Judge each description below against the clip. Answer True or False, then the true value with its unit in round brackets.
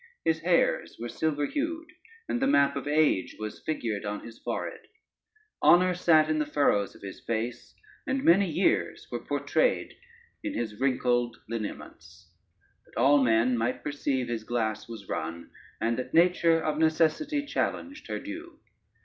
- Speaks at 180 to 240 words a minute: False (155 wpm)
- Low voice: False (145 Hz)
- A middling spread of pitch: False (7.0 semitones)